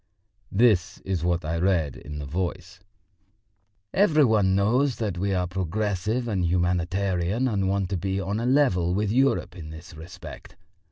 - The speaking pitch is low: Yes, very low, 95 Hz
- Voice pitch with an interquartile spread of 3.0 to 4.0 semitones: Yes, average, 3.5 semitones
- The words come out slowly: No, average, 160 wpm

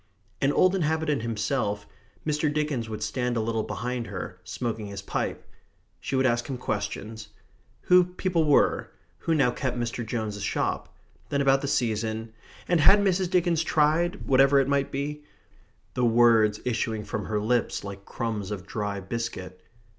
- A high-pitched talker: No, low, 120 Hz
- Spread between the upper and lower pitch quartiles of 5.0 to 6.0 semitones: Yes, average, 5.3 semitones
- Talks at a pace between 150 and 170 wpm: Yes, average, 160 wpm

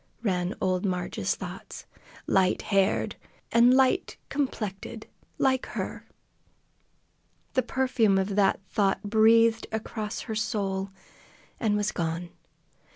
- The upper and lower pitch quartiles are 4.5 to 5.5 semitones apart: No, average, 3.1 semitones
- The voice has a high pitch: Yes, high, 210 Hz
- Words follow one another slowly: Yes, slow, 105 wpm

